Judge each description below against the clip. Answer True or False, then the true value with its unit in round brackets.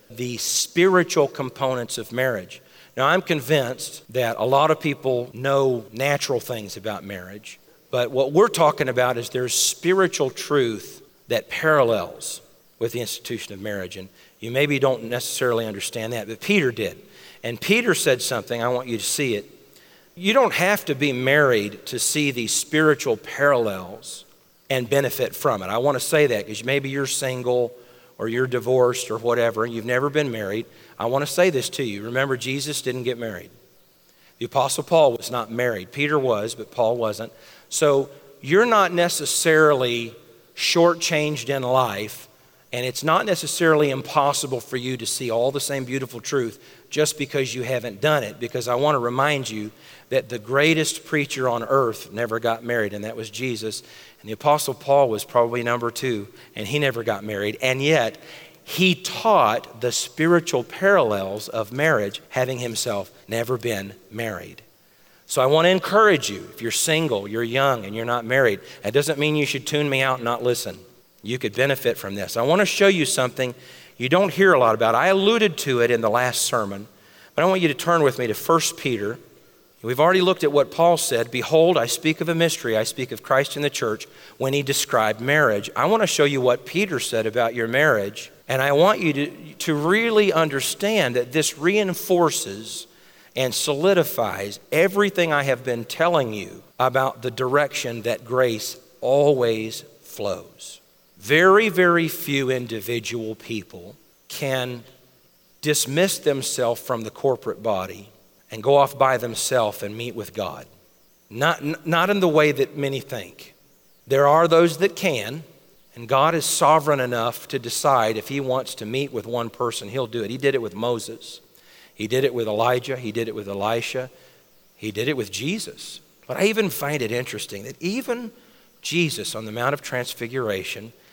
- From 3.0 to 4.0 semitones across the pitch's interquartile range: False (4.5 semitones)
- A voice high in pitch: False (130 Hz)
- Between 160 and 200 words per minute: True (180 wpm)